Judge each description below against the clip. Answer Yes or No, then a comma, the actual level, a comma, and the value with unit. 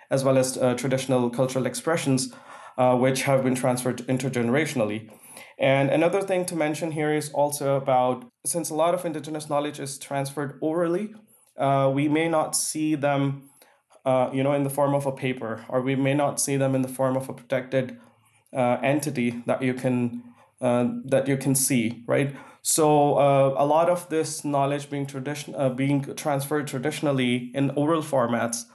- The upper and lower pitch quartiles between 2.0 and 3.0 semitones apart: Yes, narrow, 2.4 semitones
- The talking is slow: No, average, 175 wpm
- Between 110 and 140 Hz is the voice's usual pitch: Yes, low, 135 Hz